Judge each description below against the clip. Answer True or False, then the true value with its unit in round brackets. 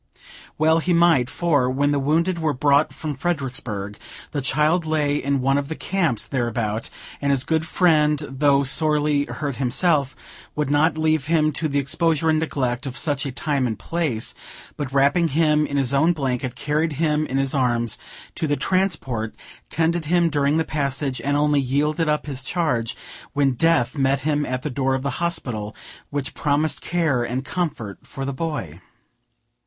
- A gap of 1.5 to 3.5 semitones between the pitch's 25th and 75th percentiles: True (3.0 semitones)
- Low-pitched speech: False (145 Hz)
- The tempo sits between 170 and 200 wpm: True (175 wpm)